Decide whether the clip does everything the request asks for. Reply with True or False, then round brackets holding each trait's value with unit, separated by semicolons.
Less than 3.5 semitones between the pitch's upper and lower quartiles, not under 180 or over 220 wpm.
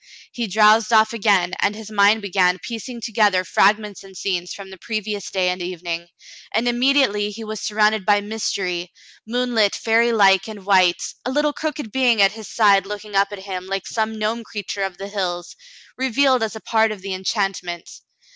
True (2.6 semitones; 185 wpm)